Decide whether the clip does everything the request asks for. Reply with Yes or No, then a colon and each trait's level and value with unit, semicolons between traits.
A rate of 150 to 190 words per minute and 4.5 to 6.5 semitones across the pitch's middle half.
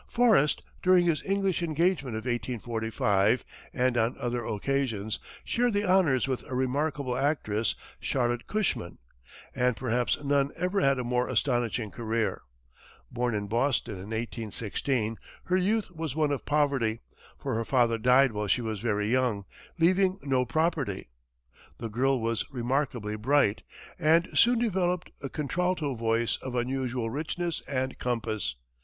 No: average, 140 wpm; average, 4.9 semitones